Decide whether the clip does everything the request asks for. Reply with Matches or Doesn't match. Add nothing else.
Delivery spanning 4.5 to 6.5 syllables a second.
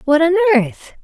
Matches